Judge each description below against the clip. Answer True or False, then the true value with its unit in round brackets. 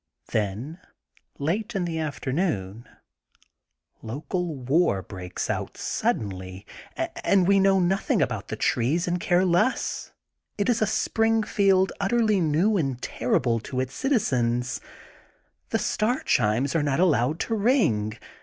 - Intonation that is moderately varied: False (8.4 semitones)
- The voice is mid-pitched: True (165 Hz)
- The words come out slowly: True (130 wpm)